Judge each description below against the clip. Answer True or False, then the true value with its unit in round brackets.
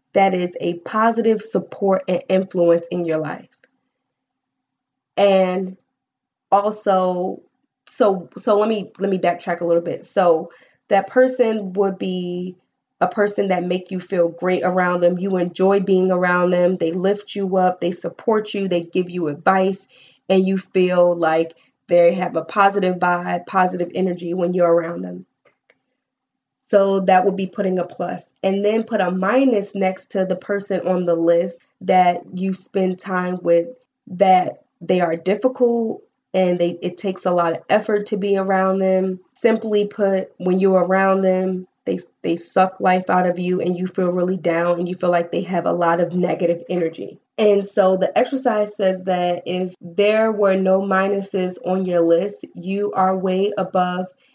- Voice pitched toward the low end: False (185 Hz)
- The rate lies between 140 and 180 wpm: True (170 wpm)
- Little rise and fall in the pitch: True (2.0 semitones)